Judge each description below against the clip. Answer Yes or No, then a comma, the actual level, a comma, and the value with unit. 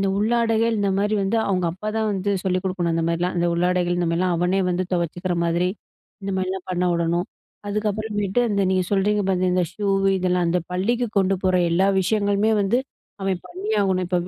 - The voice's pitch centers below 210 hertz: Yes, high, 190 Hz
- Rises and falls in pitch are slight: Yes, narrow, 2.3 semitones